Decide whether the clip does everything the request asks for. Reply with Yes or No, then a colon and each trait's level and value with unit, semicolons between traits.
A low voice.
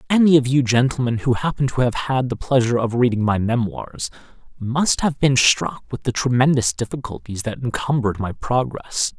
Yes: low, 125 Hz